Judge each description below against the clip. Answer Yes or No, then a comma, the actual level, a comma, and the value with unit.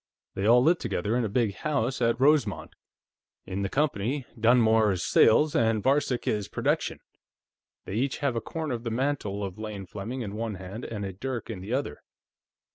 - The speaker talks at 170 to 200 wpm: Yes, average, 190 wpm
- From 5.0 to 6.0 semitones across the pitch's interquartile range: No, average, 4.3 semitones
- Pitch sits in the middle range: No, low, 115 Hz